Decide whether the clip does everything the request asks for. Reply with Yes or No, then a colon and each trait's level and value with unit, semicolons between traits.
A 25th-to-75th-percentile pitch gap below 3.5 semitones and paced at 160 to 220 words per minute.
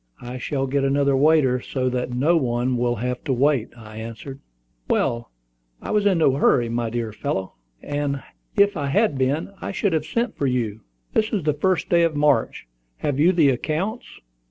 No: average, 4.3 semitones; average, 185 wpm